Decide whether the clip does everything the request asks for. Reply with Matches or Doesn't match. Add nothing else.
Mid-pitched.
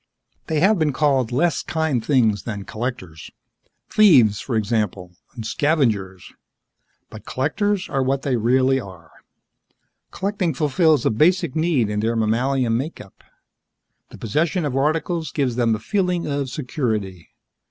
Doesn't match